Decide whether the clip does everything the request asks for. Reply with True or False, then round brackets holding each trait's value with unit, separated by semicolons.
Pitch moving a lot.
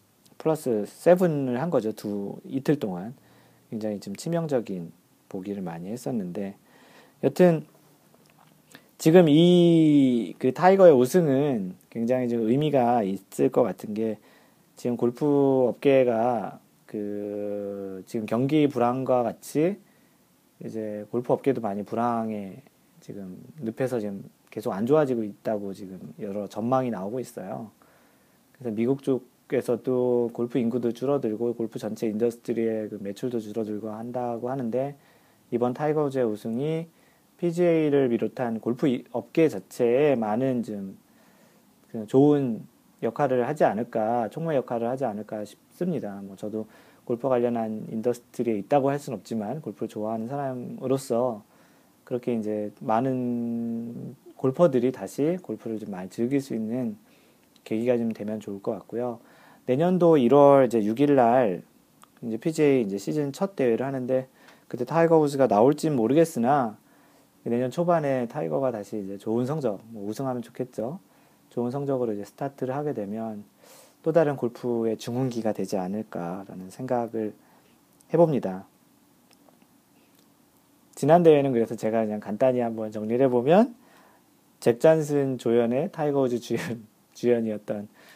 False (4.2 semitones)